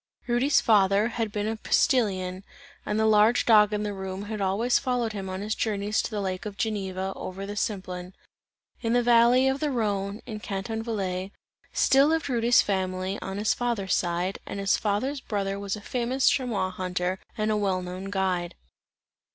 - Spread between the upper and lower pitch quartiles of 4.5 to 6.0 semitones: No, average, 3.1 semitones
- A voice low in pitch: No, high, 205 Hz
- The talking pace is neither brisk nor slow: Yes, average, 185 wpm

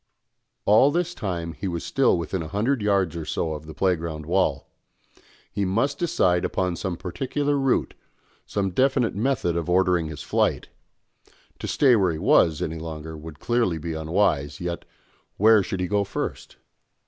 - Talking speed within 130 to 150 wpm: No, average, 165 wpm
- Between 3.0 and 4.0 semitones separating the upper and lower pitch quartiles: No, average, 5.0 semitones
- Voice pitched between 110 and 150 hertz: No, very low, 90 Hz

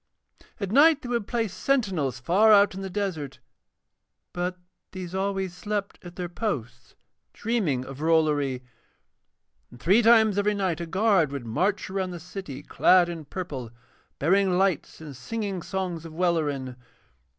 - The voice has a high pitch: No, medium, 180 Hz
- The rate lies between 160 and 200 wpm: No, average, 150 wpm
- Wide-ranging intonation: No, average, 4.6 semitones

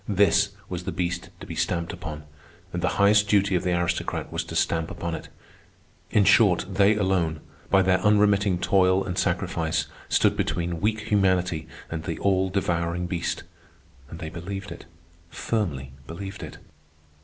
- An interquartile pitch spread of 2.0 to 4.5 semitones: Yes, average, 2.8 semitones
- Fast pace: No, average, 160 wpm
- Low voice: Yes, very low, 95 Hz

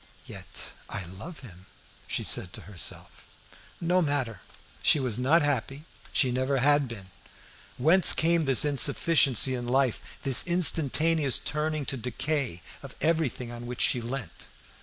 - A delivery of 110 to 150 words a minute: Yes, average, 140 wpm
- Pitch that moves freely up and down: No, average, 4.1 semitones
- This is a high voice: No, low, 135 Hz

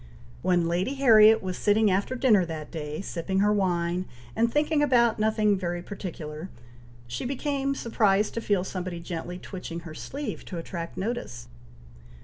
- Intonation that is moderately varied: Yes, average, 4.6 semitones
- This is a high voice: Yes, high, 195 Hz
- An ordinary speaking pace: Yes, average, 155 wpm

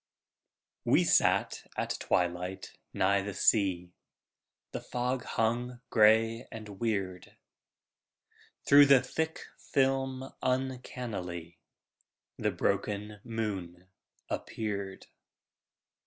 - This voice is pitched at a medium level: No, low, 110 Hz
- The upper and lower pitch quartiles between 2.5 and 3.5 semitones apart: No, average, 4.8 semitones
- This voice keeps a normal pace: No, slow, 80 wpm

